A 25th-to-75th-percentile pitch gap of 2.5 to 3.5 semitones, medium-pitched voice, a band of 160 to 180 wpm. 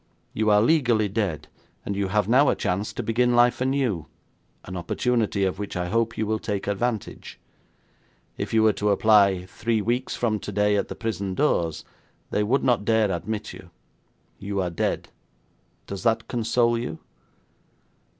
No: average, 2.9 semitones; low, 110 Hz; average, 165 wpm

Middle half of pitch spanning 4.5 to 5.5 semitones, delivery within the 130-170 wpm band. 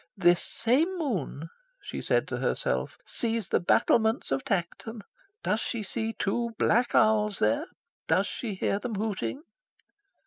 No: average, 3.1 semitones; average, 140 wpm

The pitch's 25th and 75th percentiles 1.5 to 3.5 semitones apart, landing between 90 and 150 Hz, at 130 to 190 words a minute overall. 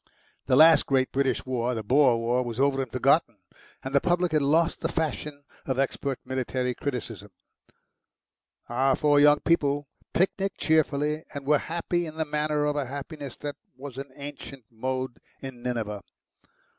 Yes: average, 2.7 semitones; medium, 140 Hz; average, 160 wpm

